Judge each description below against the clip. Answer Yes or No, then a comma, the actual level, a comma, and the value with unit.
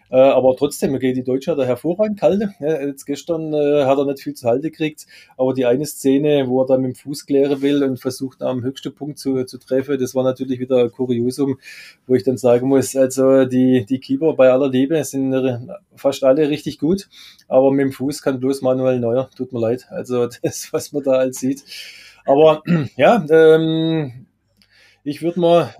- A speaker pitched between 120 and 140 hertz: Yes, low, 135 Hz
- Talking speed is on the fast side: Yes, fast, 200 wpm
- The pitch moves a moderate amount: No, narrow, 2.1 semitones